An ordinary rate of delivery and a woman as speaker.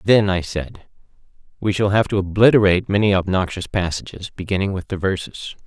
No: average, 160 wpm; male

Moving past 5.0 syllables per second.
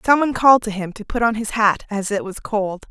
Yes: 5.9 syllables/s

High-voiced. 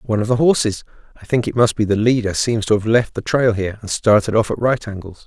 No: low, 110 Hz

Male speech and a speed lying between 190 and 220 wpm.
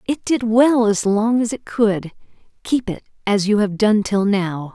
No: female; average, 200 wpm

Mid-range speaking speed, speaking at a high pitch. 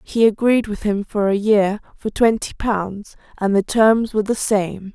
Yes: average, 195 wpm; high, 210 Hz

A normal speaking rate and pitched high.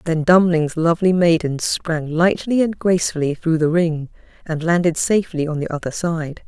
No: average, 165 wpm; medium, 165 Hz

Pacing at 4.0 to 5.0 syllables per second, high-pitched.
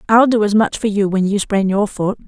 No: 5.5 syllables/s; high, 205 Hz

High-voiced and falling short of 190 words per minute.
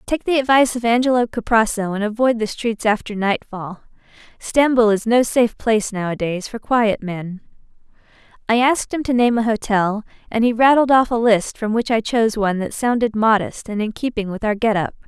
No: high, 225 Hz; average, 195 wpm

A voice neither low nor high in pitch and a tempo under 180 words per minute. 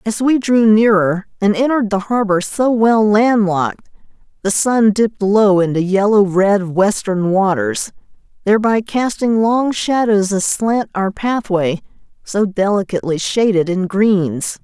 No: high, 205 Hz; slow, 135 wpm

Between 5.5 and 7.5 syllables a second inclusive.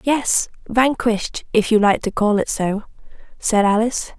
No: 4.6 syllables/s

